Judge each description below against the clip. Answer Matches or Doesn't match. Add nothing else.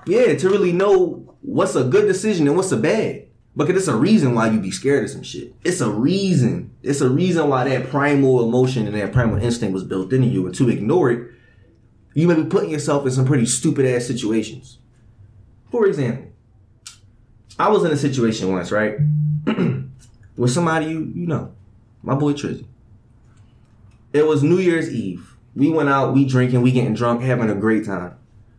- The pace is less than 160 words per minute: Doesn't match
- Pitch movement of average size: Matches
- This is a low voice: Matches